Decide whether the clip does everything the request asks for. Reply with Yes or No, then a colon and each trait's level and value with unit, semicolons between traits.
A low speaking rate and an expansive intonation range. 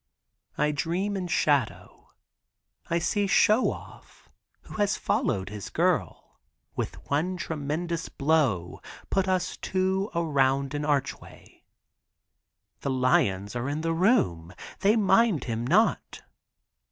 Yes: slow, 115 wpm; wide, 6.1 semitones